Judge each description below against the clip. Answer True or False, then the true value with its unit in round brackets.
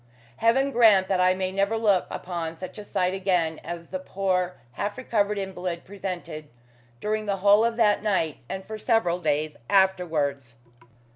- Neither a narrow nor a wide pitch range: True (3.0 semitones)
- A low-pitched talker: False (190 Hz)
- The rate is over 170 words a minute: False (160 wpm)